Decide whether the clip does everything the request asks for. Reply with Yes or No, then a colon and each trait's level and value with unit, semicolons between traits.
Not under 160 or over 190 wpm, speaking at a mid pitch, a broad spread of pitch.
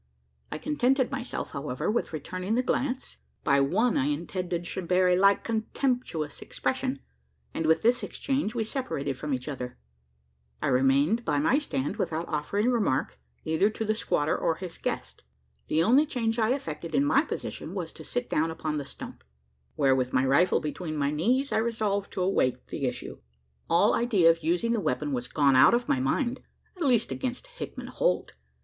Yes: average, 180 wpm; medium, 180 Hz; wide, 8.2 semitones